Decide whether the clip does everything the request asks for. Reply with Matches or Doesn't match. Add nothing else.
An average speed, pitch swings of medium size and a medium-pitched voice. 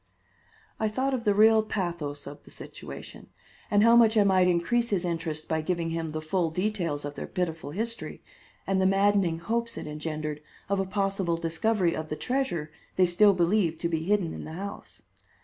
Matches